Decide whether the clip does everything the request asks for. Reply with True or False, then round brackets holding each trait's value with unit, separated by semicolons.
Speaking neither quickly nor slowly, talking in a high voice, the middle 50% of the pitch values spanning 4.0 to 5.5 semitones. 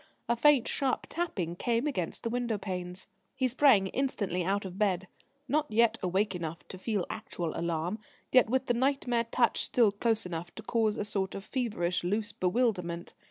True (175 wpm; 210 Hz; 5.0 semitones)